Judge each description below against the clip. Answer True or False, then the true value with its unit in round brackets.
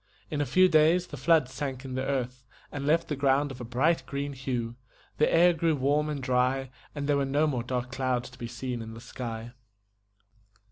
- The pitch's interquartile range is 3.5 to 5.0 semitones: False (2.8 semitones)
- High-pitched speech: False (135 Hz)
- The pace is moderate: False (215 wpm)